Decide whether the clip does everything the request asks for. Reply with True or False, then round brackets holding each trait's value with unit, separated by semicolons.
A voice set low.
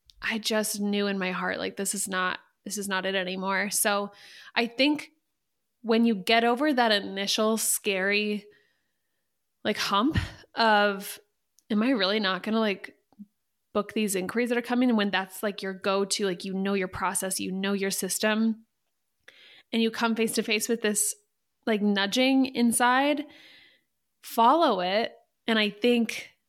False (215 Hz)